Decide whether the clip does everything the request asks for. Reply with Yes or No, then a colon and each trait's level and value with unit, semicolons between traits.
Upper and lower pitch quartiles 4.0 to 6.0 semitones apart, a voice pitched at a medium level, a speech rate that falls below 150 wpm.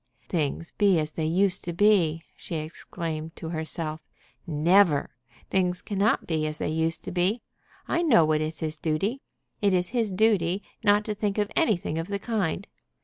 No: average, 4.3 semitones; medium, 175 Hz; average, 175 wpm